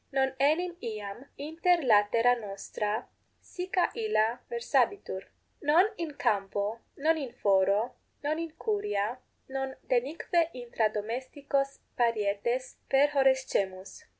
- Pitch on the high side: Yes, very high, 260 Hz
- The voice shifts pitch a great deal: Yes, wide, 6.4 semitones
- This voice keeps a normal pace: No, slow, 100 wpm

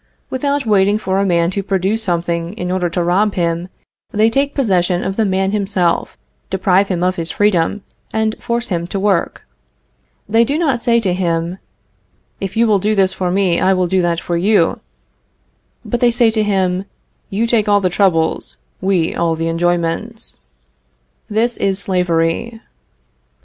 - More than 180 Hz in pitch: Yes, high, 190 Hz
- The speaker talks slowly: No, average, 170 wpm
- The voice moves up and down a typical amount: Yes, average, 3.6 semitones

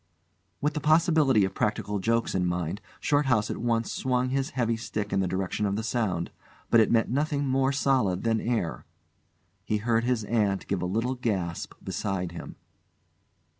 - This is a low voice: Yes, low, 115 Hz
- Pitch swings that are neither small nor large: Yes, average, 4.8 semitones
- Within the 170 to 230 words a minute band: Yes, average, 175 wpm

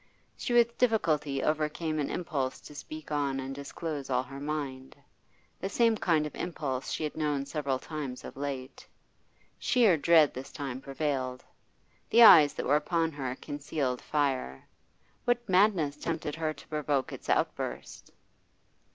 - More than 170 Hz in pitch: No, medium, 150 Hz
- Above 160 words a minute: No, average, 150 wpm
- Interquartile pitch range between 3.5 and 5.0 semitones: No, average, 2.9 semitones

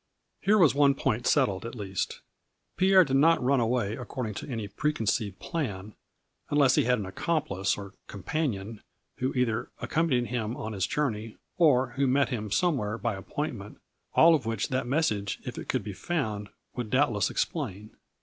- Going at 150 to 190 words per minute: Yes, average, 175 wpm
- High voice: No, low, 120 Hz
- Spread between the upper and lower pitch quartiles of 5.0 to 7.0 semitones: Yes, average, 5.3 semitones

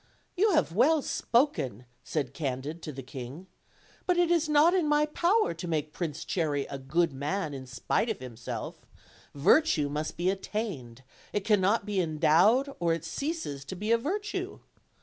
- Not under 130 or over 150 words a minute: No, average, 170 wpm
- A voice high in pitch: No, medium, 175 Hz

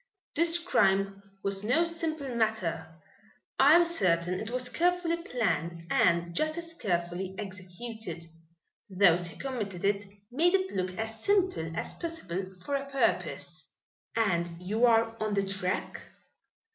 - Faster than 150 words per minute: No, slow, 135 wpm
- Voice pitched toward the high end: Yes, high, 215 Hz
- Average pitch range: No, wide, 8.1 semitones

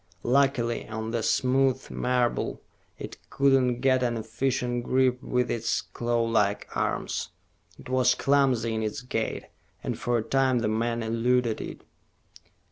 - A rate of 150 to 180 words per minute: No, average, 140 wpm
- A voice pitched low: Yes, low, 120 Hz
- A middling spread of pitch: No, narrow, 2.1 semitones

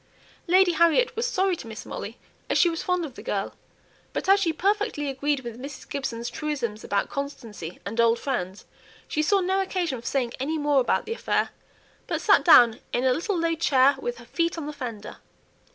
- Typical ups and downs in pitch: No, wide, 6.3 semitones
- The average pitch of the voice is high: Yes, very high, 290 Hz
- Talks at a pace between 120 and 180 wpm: No, average, 200 wpm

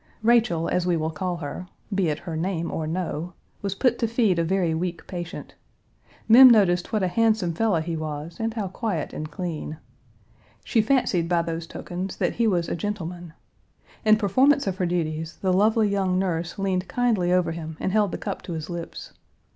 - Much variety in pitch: No, average, 3.9 semitones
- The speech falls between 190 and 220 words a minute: Yes, average, 195 wpm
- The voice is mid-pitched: Yes, medium, 180 Hz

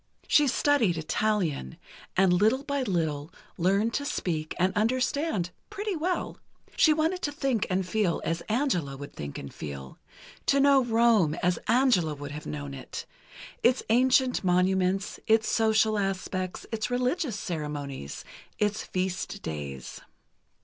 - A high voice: Yes, high, 200 Hz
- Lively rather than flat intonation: Yes, wide, 7.4 semitones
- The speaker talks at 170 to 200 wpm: No, slow, 135 wpm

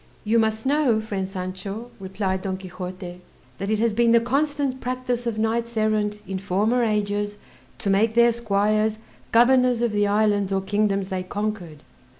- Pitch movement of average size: Yes, average, 3.0 semitones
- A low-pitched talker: No, high, 215 Hz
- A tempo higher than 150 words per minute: Yes, average, 160 wpm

